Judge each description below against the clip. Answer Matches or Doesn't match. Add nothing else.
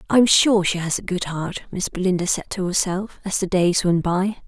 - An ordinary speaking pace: Doesn't match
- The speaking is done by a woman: Matches